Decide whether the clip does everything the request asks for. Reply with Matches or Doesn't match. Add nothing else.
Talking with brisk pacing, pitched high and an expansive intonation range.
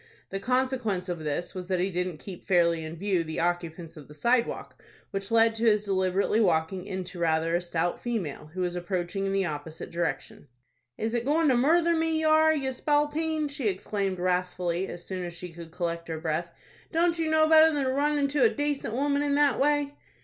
Matches